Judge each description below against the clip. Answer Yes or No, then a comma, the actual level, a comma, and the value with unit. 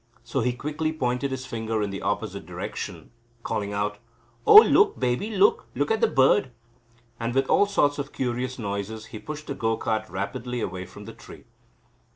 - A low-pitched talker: Yes, low, 125 Hz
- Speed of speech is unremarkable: Yes, average, 185 wpm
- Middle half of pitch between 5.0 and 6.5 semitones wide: Yes, wide, 5.5 semitones